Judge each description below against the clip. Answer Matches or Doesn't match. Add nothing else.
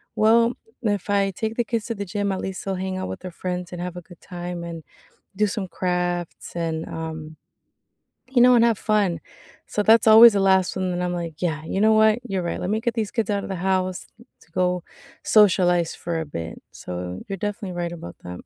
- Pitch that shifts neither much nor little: Matches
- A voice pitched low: Doesn't match